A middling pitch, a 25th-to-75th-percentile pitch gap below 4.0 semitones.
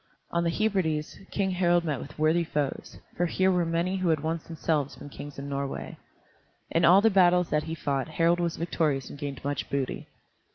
Yes: medium, 165 Hz; average, 3.2 semitones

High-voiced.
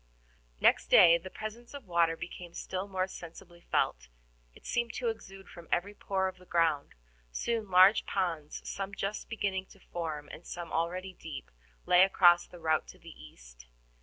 No: medium, 180 Hz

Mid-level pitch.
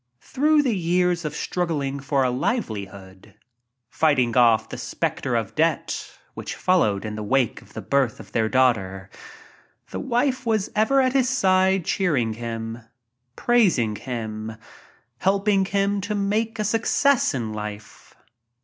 Yes: medium, 150 Hz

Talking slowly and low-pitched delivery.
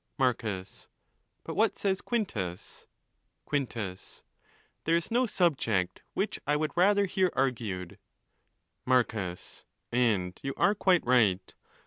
Yes: slow, 95 wpm; low, 125 Hz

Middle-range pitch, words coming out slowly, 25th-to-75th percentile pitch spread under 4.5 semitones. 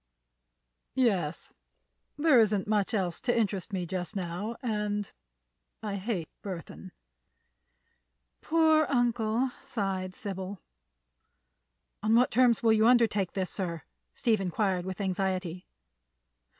No: high, 205 Hz; slow, 105 wpm; average, 3.8 semitones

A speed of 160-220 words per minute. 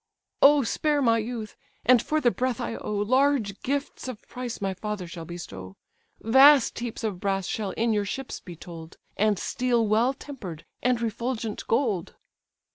Yes: average, 165 wpm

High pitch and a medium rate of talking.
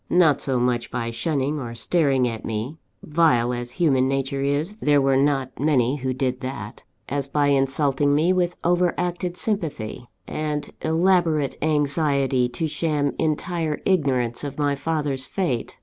No: medium, 145 Hz; average, 150 wpm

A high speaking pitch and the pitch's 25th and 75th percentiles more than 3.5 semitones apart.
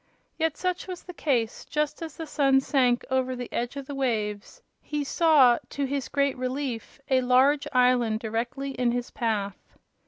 No: very high, 260 Hz; average, 2.9 semitones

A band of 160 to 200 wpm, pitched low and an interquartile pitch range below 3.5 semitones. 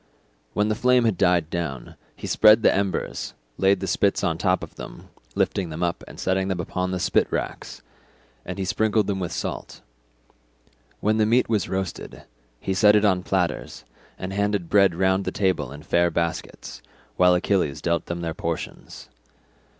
Yes: average, 175 wpm; very low, 95 Hz; average, 3.0 semitones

